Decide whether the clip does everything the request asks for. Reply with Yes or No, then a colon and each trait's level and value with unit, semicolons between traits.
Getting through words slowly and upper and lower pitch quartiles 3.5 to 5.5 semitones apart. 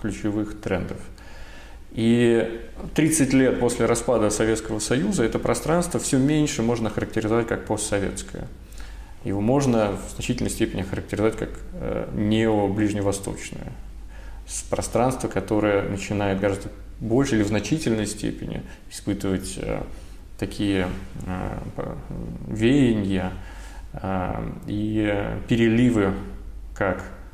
No: slow, 90 wpm; average, 3.0 semitones